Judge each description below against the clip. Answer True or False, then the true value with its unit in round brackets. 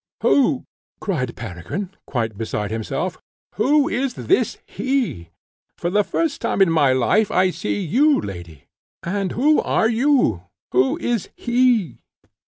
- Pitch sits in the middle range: False (195 Hz)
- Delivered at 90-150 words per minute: True (140 wpm)